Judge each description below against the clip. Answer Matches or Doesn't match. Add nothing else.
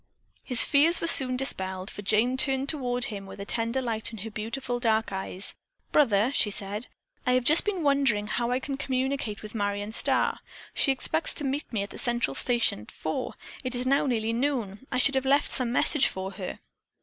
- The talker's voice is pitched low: Doesn't match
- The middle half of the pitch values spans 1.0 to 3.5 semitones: Doesn't match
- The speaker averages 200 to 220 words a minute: Matches